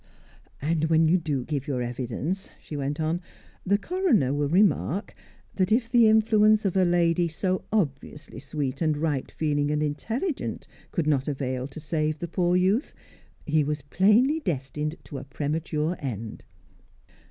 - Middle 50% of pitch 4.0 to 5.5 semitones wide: Yes, average, 4.6 semitones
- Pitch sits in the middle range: Yes, medium, 155 Hz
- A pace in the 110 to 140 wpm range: No, average, 155 wpm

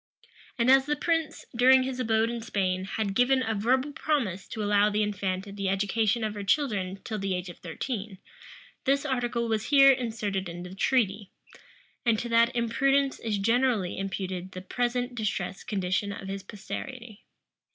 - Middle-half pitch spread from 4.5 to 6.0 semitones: No, average, 4.1 semitones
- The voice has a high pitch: Yes, high, 220 Hz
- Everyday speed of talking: Yes, average, 170 wpm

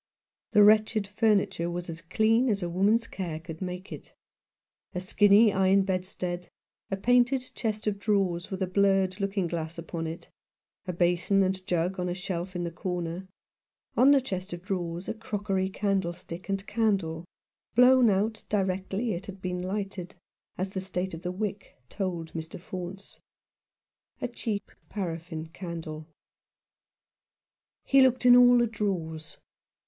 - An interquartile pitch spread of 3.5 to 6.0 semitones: No, average, 2.9 semitones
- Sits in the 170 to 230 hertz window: Yes, high, 190 Hz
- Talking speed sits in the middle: Yes, average, 155 wpm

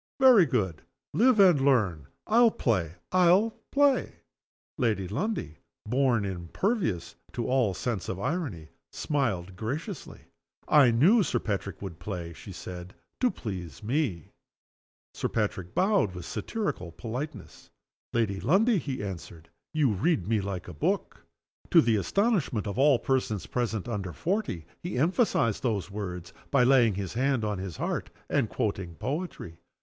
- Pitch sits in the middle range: No, low, 115 Hz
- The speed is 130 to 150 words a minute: Yes, average, 140 wpm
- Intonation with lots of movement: Yes, wide, 8.8 semitones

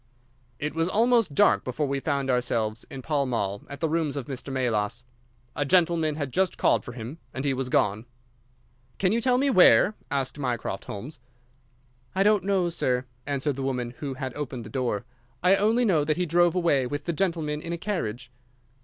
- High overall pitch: No, medium, 145 Hz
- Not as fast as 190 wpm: No, average, 195 wpm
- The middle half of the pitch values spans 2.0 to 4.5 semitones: No, average, 5.3 semitones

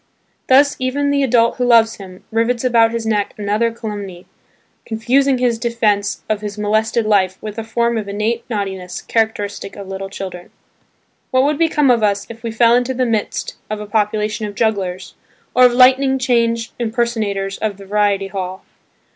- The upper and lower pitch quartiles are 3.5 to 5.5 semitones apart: No, average, 2.8 semitones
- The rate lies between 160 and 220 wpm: Yes, average, 170 wpm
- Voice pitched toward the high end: Yes, high, 220 Hz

